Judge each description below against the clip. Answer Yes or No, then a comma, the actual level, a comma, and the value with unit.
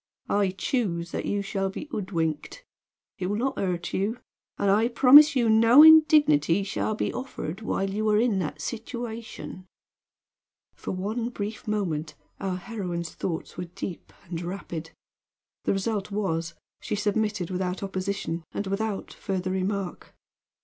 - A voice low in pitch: No, high, 200 Hz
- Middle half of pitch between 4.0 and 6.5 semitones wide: No, average, 3.3 semitones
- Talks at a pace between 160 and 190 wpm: No, average, 140 wpm